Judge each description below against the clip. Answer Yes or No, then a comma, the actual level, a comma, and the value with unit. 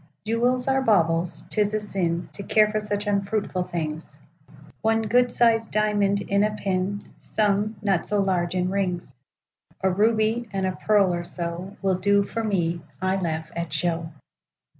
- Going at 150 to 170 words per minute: No, average, 140 wpm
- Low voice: No, high, 200 Hz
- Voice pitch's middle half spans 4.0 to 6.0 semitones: No, average, 3.2 semitones